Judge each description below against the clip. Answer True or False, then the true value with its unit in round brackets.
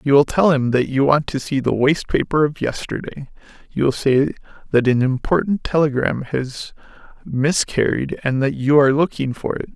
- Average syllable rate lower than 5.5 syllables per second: True (5.0 syllables/s)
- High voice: False (140 Hz)